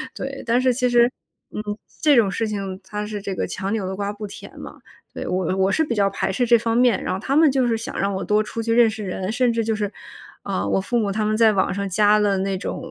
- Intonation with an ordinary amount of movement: Yes, average, 3.2 semitones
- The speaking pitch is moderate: No, high, 215 Hz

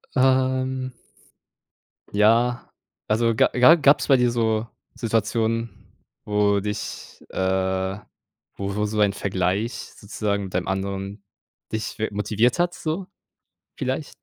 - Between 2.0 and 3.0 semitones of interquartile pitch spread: No, average, 3.6 semitones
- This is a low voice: Yes, low, 110 Hz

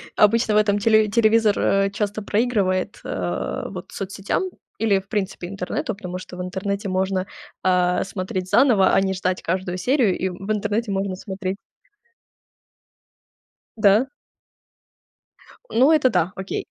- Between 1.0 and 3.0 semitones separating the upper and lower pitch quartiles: Yes, narrow, 2.5 semitones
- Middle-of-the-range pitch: No, high, 195 Hz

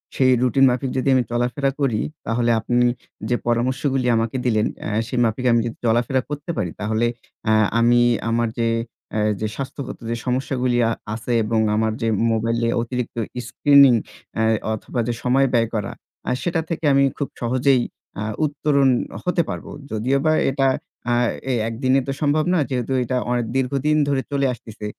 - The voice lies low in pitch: Yes, low, 125 Hz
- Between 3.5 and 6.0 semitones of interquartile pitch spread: No, average, 2.9 semitones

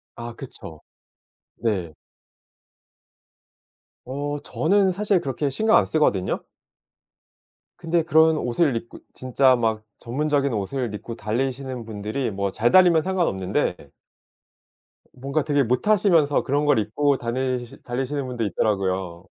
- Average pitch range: Yes, average, 5.0 semitones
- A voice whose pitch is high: No, low, 130 Hz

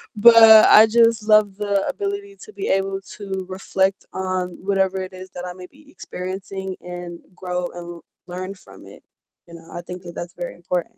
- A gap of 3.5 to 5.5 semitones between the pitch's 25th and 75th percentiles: No, narrow, 2.4 semitones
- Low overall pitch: No, high, 190 Hz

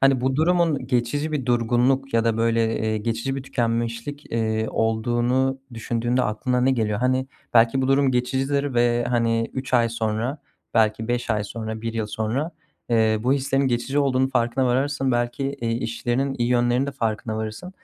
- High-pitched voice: No, low, 120 Hz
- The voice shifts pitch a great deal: No, narrow, 2.6 semitones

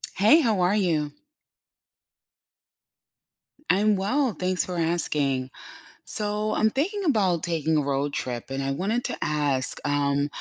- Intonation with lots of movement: Yes, wide, 6.7 semitones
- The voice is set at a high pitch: No, medium, 175 Hz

